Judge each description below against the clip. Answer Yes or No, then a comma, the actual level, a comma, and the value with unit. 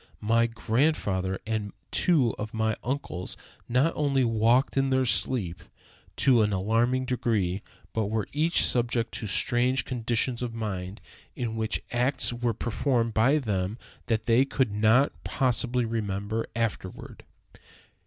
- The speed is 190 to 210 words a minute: No, slow, 135 wpm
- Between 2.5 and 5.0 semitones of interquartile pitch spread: Yes, average, 2.9 semitones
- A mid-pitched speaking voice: No, low, 115 Hz